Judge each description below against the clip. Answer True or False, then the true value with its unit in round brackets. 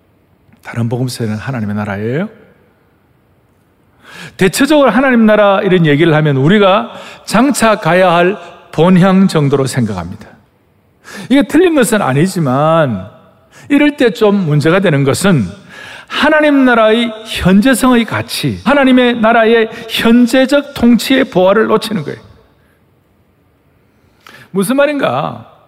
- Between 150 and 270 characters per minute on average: True (255 characters per minute)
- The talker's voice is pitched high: True (195 Hz)